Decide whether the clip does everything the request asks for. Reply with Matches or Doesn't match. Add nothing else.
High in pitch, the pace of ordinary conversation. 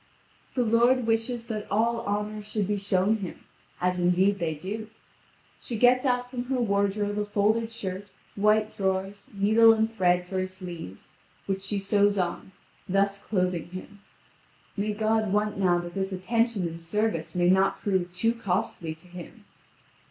Matches